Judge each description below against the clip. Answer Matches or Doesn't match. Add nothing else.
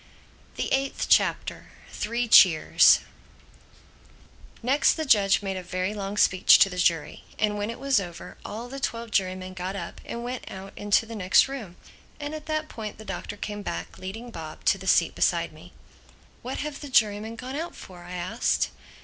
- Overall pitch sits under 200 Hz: Doesn't match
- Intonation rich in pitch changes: Doesn't match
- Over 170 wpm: Matches